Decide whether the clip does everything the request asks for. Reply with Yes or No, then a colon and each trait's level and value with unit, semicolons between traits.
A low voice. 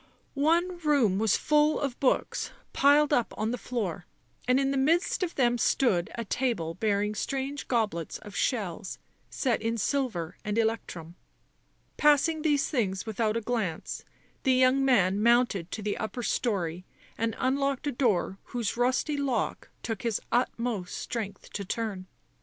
No: high, 235 Hz